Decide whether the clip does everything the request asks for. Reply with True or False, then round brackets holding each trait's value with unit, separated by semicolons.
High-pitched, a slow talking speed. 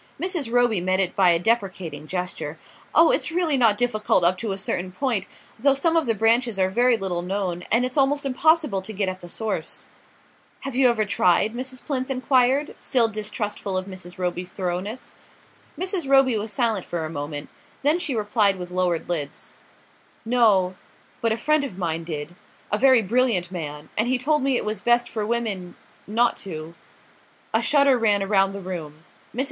False (215 Hz; 185 wpm)